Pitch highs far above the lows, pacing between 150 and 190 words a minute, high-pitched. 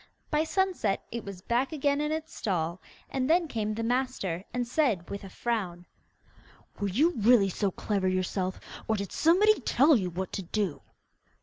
Yes: wide, 6.9 semitones; average, 175 wpm; high, 220 Hz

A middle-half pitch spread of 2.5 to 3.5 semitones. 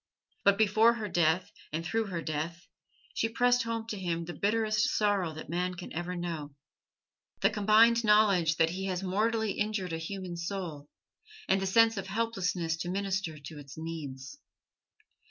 No: average, 4.4 semitones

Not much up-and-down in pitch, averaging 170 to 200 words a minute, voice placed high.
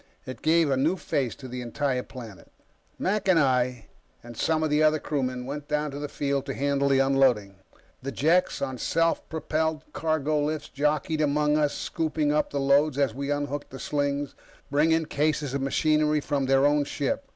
No: narrow, 2.2 semitones; average, 185 wpm; medium, 145 Hz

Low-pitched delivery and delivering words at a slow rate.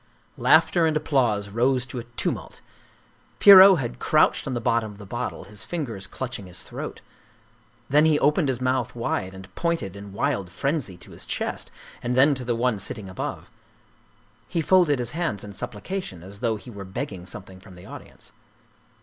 No: low, 120 Hz; average, 180 wpm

